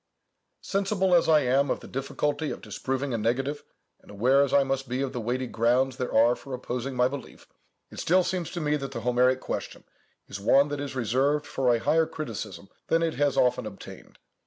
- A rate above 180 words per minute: Yes, fast, 205 wpm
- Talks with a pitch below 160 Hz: Yes, low, 135 Hz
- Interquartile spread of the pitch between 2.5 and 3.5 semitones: Yes, average, 2.9 semitones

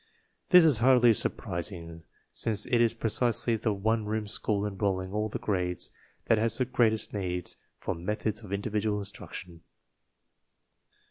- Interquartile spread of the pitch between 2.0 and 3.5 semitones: Yes, average, 2.7 semitones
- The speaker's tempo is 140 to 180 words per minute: Yes, average, 150 wpm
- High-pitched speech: No, low, 105 Hz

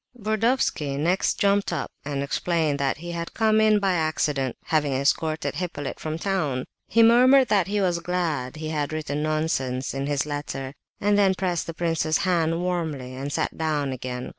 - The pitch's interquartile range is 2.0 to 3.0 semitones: No, average, 4.5 semitones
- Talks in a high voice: No, medium, 160 Hz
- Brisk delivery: No, average, 175 wpm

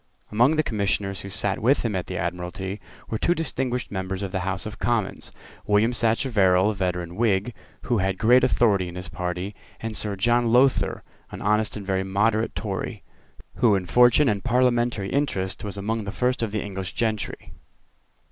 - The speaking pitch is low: Yes, low, 105 Hz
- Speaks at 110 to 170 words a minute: No, average, 180 wpm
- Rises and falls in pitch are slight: No, average, 3.8 semitones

